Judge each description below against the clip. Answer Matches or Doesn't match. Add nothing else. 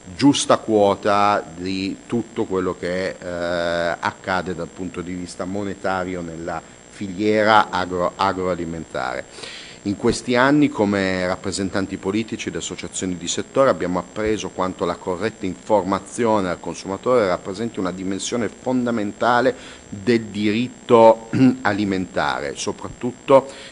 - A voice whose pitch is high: Doesn't match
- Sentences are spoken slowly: Matches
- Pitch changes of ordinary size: Matches